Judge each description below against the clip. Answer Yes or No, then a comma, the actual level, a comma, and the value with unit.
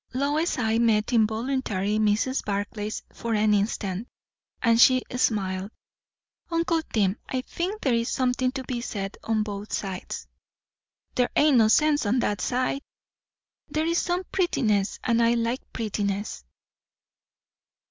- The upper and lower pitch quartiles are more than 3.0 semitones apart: Yes, average, 3.8 semitones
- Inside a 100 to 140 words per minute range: Yes, slow, 135 wpm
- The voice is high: Yes, high, 230 Hz